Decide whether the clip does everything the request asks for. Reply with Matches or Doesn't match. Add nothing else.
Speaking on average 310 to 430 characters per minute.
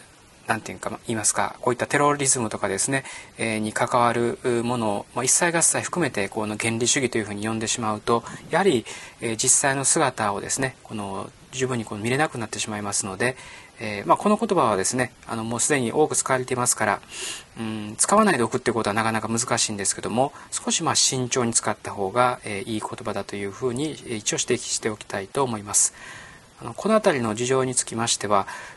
Matches